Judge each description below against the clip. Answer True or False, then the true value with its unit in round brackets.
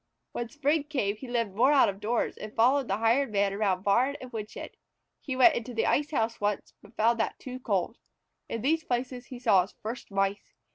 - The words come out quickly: True (210 wpm)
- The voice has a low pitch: False (235 Hz)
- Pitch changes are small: False (4.0 semitones)